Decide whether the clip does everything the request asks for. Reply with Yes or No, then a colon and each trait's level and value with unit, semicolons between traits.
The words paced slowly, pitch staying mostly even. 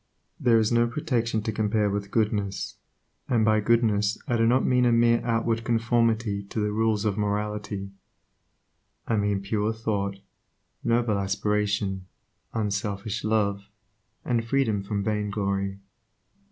Yes: slow, 130 wpm; narrow, 2.1 semitones